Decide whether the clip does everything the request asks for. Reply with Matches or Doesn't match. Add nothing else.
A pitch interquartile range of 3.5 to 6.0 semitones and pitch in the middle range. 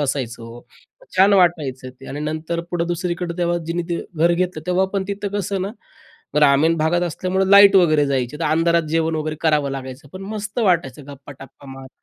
Matches